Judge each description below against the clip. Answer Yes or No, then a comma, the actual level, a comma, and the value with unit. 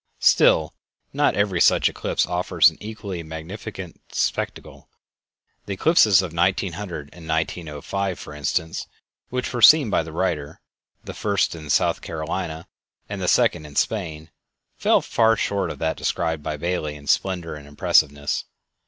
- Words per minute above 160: No, average, 145 wpm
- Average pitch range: Yes, average, 4.0 semitones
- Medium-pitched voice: No, very low, 85 Hz